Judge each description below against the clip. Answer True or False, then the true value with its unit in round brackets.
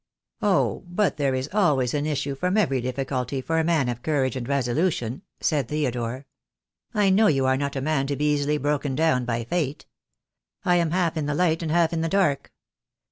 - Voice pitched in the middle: True (145 Hz)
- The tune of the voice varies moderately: True (3.8 semitones)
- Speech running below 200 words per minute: False (205 wpm)